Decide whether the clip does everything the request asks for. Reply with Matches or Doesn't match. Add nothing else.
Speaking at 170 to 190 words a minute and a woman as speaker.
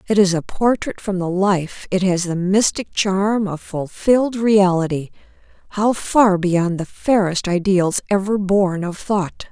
Doesn't match